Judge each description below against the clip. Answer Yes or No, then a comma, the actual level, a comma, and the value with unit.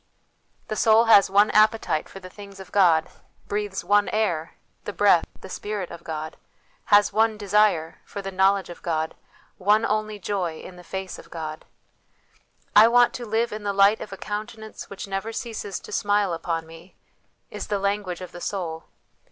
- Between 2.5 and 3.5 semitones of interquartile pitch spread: Yes, average, 3.0 semitones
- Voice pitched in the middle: No, high, 200 Hz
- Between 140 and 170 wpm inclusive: No, average, 185 wpm